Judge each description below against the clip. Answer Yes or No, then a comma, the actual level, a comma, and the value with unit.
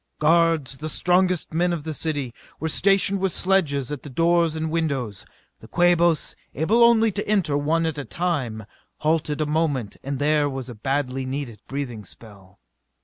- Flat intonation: No, average, 4.0 semitones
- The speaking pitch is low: No, medium, 155 Hz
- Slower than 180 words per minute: Yes, average, 170 wpm